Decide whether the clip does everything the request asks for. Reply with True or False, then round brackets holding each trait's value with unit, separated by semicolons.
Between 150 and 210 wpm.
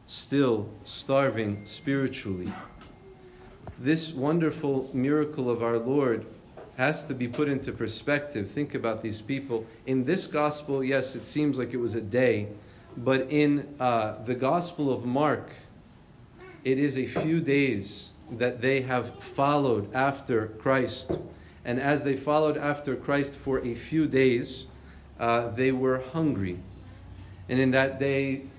False (140 wpm)